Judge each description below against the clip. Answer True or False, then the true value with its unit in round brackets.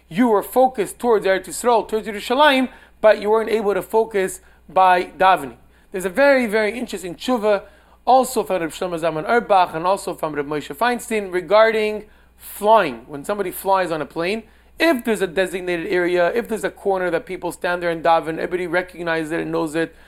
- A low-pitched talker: False (190 Hz)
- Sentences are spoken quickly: False (190 wpm)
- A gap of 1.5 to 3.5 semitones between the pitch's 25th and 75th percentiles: False (4.0 semitones)